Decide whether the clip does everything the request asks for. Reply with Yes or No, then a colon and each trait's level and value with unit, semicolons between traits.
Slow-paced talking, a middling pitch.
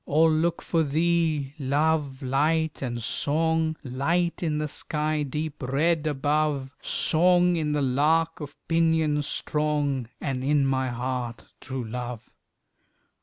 Yes: slow, 125 wpm; medium, 150 Hz